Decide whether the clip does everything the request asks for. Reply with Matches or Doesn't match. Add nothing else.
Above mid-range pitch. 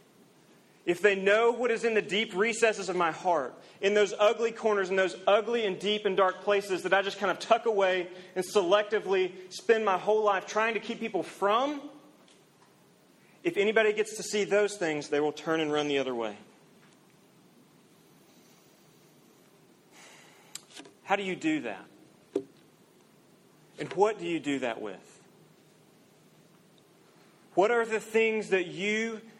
Matches